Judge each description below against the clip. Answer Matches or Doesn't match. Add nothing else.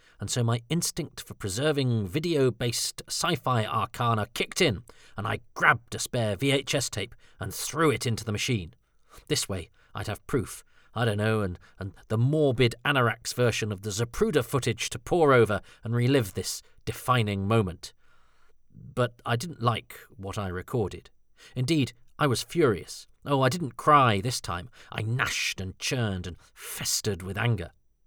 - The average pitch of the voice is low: Matches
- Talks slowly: Doesn't match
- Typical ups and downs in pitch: Matches